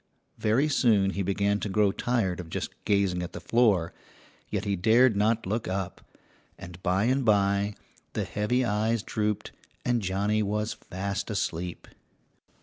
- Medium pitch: No, low, 105 Hz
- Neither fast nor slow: Yes, average, 150 wpm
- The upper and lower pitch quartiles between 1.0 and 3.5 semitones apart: Yes, narrow, 2.4 semitones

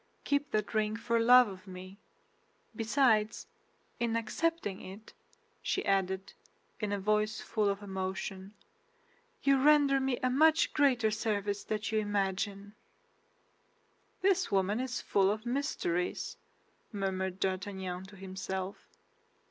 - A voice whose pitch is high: Yes, high, 210 Hz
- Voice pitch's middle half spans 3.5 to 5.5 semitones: Yes, average, 4.1 semitones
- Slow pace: Yes, slow, 120 wpm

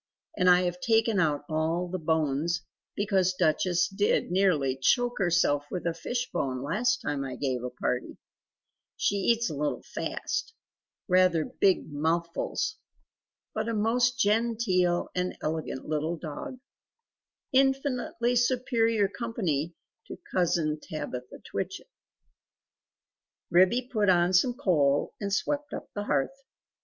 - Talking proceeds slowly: Yes, slow, 125 wpm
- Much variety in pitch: Yes, wide, 6.4 semitones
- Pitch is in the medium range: Yes, medium, 180 Hz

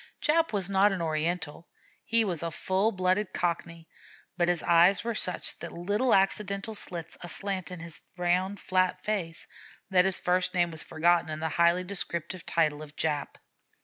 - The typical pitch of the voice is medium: Yes, medium, 180 Hz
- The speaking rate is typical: Yes, average, 165 wpm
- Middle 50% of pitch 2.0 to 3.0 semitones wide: Yes, narrow, 2.5 semitones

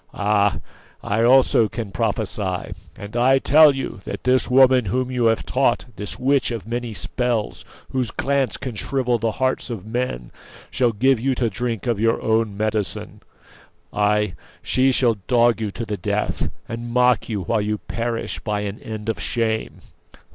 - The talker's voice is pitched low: Yes, low, 115 Hz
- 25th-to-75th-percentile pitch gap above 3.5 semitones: No, average, 3.1 semitones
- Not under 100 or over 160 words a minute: No, average, 170 wpm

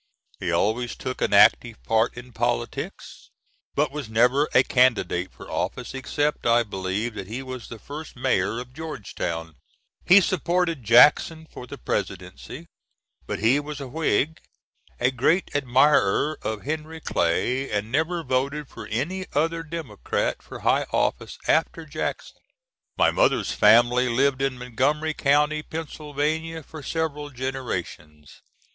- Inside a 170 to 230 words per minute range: No, average, 140 wpm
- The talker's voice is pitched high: No, low, 135 Hz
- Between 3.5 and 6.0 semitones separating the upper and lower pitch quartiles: Yes, average, 4.6 semitones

